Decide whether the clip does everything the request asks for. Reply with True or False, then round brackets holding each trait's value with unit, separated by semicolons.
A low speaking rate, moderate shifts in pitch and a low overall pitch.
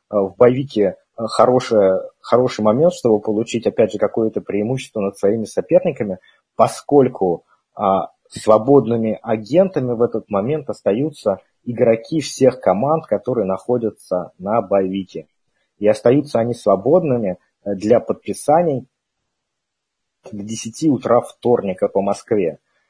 True (105 wpm; 4.0 semitones; 115 Hz)